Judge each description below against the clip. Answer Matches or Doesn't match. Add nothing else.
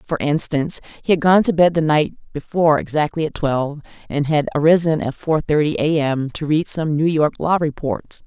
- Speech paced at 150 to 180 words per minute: Doesn't match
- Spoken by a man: Doesn't match